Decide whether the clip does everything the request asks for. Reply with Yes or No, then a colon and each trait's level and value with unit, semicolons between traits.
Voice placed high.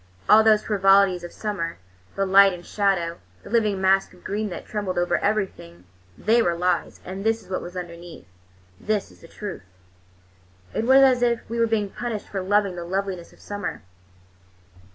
Yes: high, 195 Hz